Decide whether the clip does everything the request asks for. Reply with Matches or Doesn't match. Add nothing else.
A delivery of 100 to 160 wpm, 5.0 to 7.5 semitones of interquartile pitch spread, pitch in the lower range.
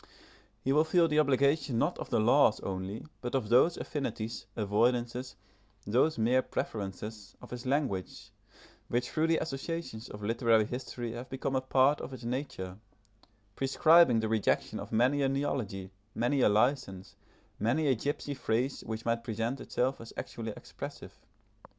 Doesn't match